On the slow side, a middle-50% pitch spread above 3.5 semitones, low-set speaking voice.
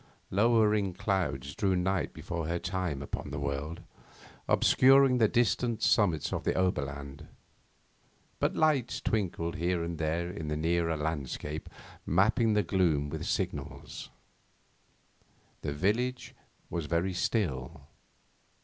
Yes: slow, 120 wpm; average, 5.1 semitones; very low, 85 Hz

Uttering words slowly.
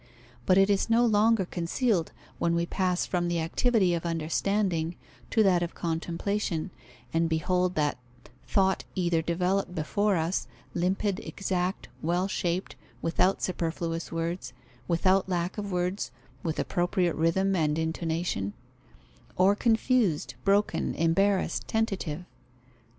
Yes: slow, 125 wpm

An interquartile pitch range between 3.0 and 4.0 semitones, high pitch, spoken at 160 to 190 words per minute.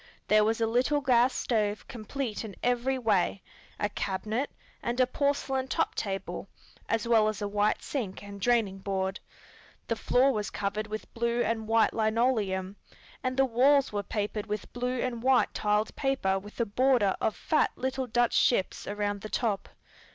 Yes: average, 3.3 semitones; high, 225 Hz; average, 170 wpm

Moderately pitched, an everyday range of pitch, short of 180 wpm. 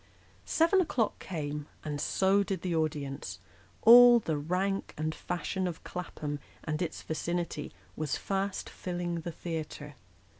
Yes: medium, 170 Hz; average, 4.0 semitones; slow, 135 wpm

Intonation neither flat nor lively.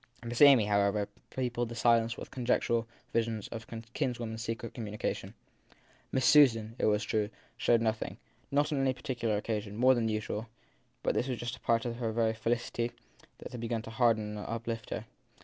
No: narrow, 1.5 semitones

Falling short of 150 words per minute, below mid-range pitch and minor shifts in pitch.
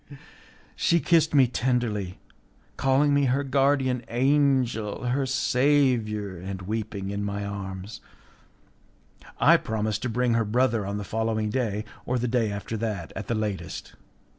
No: average, 140 wpm; low, 115 Hz; average, 4.1 semitones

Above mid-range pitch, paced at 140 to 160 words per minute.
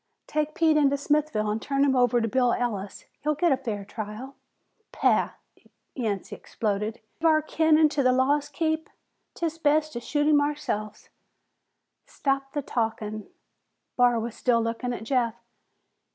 Yes: very high, 260 Hz; average, 150 wpm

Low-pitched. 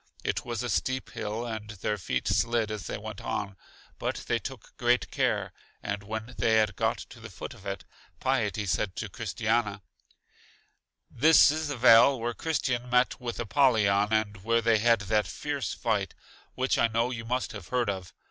Yes: low, 115 Hz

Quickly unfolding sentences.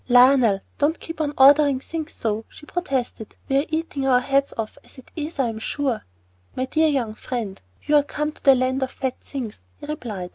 Yes: fast, 210 wpm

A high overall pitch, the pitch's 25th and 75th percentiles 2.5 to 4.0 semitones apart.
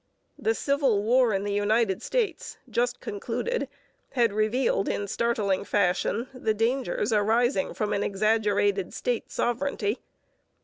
Yes: high, 225 Hz; average, 3.3 semitones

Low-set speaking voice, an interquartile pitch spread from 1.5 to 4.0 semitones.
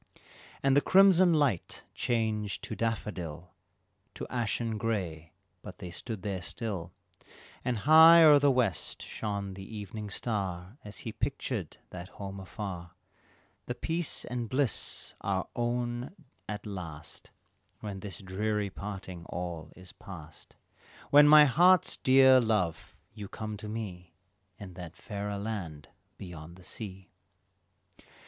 No: low, 105 Hz; average, 4.8 semitones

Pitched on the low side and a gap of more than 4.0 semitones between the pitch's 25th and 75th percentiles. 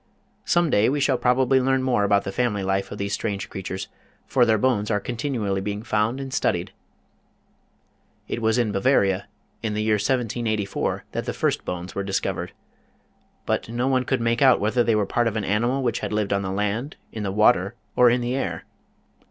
No: low, 110 Hz; average, 3.7 semitones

